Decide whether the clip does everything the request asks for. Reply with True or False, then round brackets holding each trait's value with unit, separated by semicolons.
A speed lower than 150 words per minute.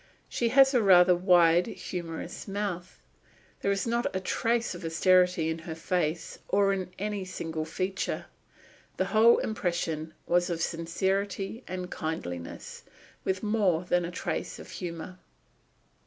True (140 wpm)